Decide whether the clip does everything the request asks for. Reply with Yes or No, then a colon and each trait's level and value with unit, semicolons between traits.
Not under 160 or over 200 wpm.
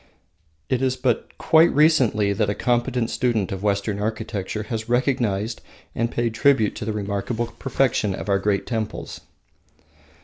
No: average, 145 wpm